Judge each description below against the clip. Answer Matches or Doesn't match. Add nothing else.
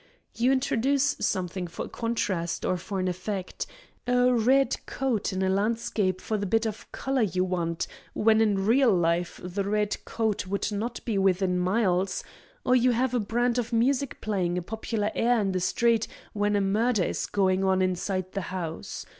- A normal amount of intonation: Matches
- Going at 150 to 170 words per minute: Doesn't match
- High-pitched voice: Matches